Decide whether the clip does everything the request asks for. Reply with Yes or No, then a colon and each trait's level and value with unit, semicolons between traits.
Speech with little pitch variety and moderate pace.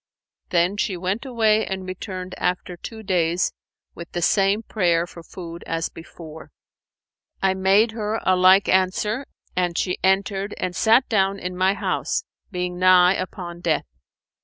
Yes: narrow, 2.0 semitones; average, 150 wpm